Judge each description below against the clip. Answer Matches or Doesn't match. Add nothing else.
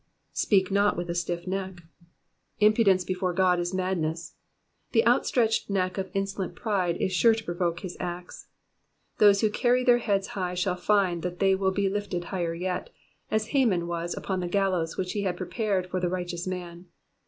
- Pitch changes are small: Matches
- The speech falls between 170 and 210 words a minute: Matches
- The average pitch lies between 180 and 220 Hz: Matches